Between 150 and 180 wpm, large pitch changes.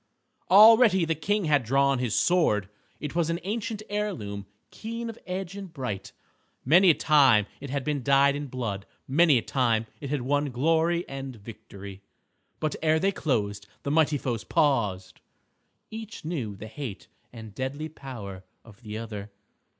Yes: average, 160 wpm; wide, 6.9 semitones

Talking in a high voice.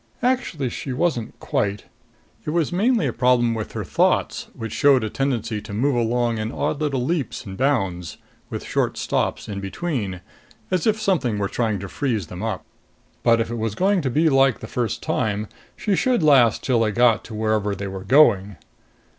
No: low, 120 Hz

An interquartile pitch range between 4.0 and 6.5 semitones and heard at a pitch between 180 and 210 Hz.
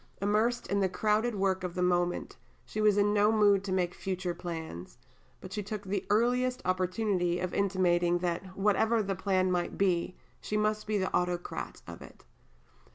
No: average, 2.8 semitones; high, 190 Hz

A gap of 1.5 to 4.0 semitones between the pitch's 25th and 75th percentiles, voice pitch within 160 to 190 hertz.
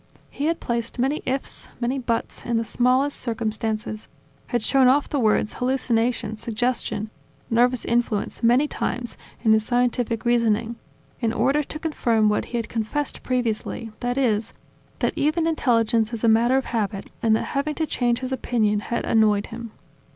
No: narrow, 2.5 semitones; high, 235 Hz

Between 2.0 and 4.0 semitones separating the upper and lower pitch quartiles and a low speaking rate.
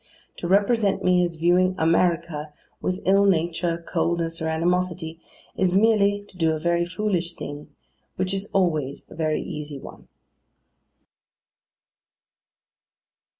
Yes: average, 2.8 semitones; slow, 120 wpm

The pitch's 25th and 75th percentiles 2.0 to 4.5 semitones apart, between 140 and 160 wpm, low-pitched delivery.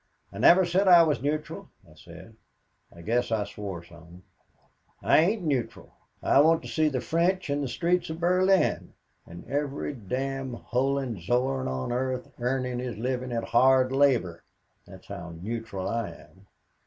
No: average, 4.9 semitones; average, 155 wpm; low, 130 Hz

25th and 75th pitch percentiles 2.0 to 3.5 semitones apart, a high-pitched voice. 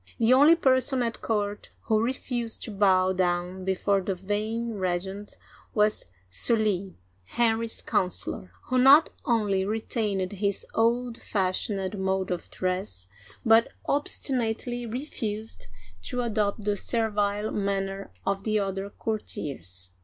Yes: average, 3.2 semitones; high, 210 Hz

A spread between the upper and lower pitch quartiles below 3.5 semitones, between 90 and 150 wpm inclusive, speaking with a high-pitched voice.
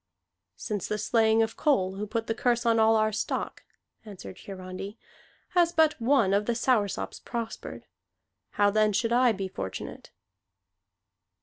Yes: average, 2.7 semitones; average, 145 wpm; high, 220 Hz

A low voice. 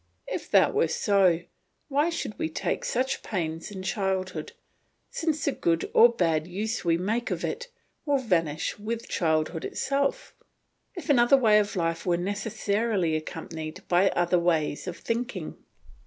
No: high, 195 Hz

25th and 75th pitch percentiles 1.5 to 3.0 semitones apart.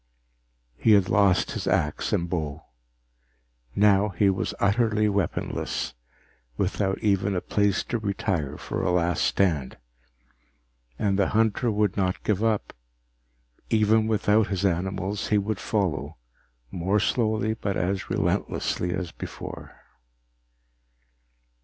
Yes: average, 2.7 semitones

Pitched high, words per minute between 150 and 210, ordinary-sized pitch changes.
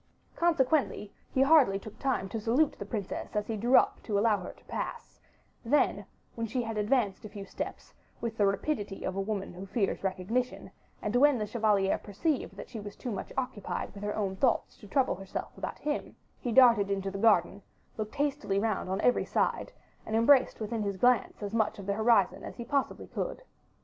Yes: high, 215 Hz; average, 200 wpm; average, 3.9 semitones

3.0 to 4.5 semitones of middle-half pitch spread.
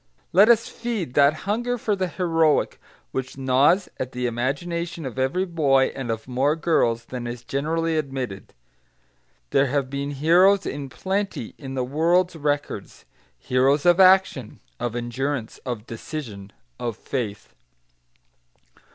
No: average, 5.3 semitones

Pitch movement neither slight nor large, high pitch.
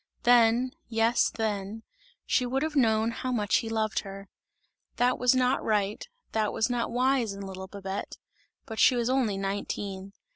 Yes: average, 3.5 semitones; high, 225 Hz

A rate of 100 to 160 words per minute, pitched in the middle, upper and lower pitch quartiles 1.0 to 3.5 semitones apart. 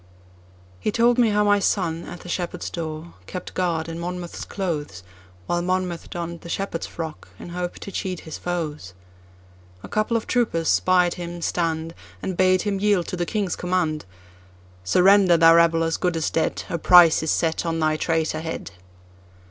Yes: average, 155 wpm; medium, 170 Hz; narrow, 2.6 semitones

